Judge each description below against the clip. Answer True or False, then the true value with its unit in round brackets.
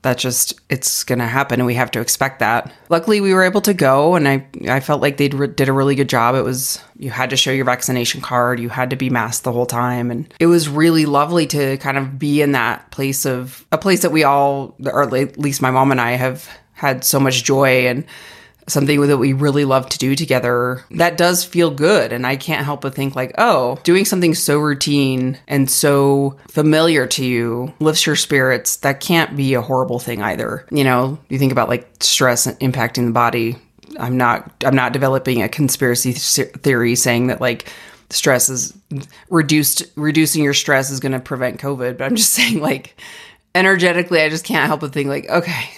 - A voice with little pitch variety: False (3.0 semitones)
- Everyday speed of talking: False (210 wpm)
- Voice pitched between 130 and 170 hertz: True (135 Hz)